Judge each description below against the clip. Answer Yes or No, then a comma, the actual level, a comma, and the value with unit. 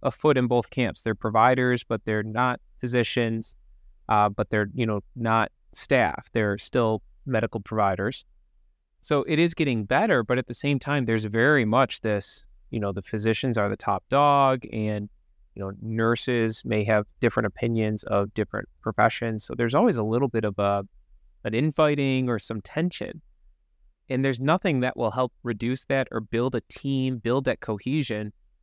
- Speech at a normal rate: Yes, average, 175 wpm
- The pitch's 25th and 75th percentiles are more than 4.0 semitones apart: No, average, 3.4 semitones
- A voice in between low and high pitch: No, low, 115 Hz